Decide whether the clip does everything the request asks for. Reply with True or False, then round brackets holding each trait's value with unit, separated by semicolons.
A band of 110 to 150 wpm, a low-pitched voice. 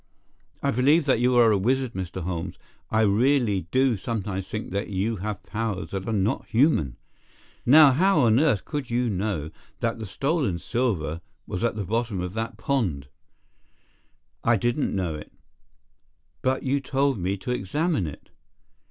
False (160 wpm; 110 Hz)